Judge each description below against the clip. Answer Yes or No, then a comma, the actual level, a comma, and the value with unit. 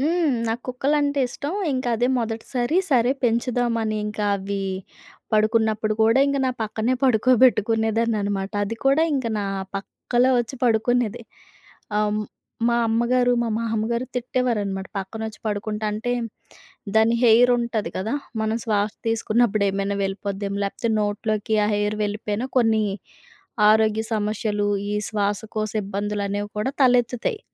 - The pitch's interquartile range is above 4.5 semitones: No, average, 2.7 semitones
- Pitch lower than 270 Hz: Yes, high, 220 Hz